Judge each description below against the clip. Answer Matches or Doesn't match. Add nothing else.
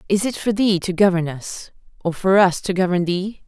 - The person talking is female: Matches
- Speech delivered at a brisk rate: Matches